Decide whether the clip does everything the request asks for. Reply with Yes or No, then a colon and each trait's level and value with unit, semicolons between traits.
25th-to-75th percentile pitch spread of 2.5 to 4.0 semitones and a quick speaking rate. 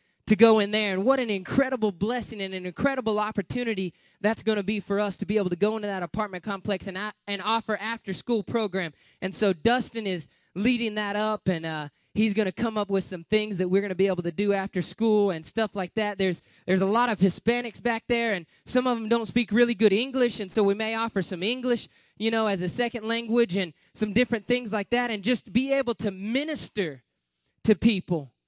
Yes: average, 3.0 semitones; fast, 230 wpm